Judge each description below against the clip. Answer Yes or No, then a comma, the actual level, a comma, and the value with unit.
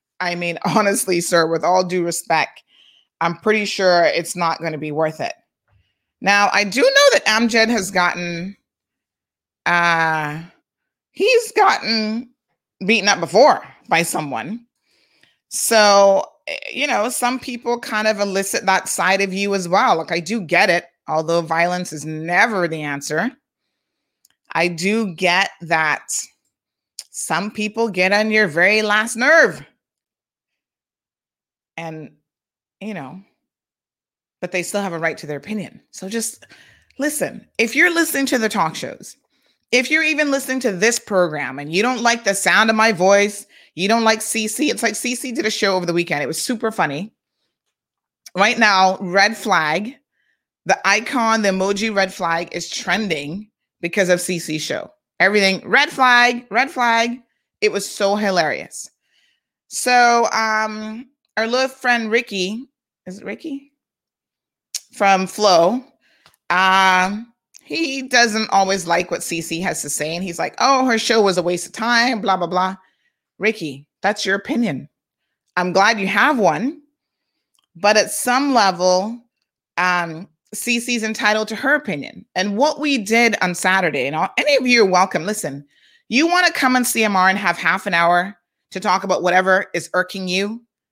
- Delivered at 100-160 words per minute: Yes, average, 155 wpm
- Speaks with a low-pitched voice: No, high, 200 Hz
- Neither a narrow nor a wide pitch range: Yes, average, 4.8 semitones